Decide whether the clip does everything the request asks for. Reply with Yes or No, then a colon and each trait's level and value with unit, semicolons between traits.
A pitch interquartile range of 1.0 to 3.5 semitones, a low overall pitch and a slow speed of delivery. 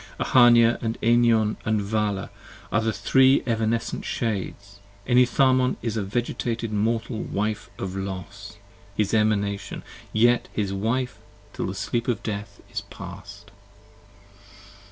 Yes: average, 2.7 semitones; low, 110 Hz; slow, 120 wpm